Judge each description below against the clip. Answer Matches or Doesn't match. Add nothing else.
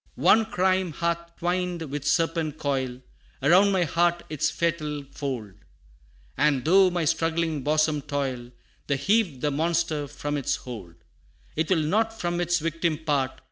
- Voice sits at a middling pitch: Matches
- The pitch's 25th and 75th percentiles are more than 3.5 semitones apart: Doesn't match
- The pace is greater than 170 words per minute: Doesn't match